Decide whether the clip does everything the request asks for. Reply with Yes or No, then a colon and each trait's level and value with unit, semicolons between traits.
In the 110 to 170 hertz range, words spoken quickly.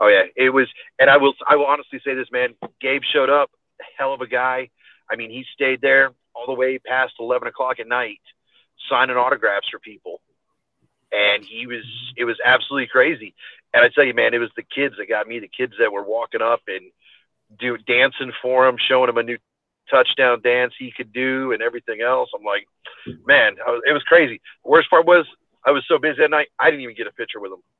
Yes: low, 130 Hz; fast, 225 wpm